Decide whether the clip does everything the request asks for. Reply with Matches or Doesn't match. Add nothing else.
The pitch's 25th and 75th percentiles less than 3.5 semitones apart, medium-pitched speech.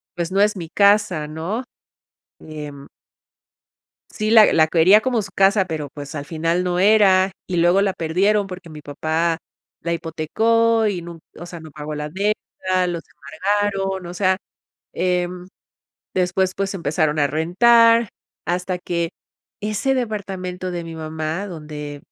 Doesn't match